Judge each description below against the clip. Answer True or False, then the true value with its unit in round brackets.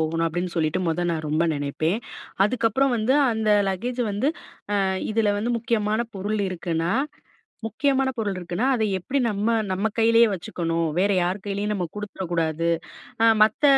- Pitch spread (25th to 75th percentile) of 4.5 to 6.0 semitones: True (4.8 semitones)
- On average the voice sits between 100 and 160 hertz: False (205 Hz)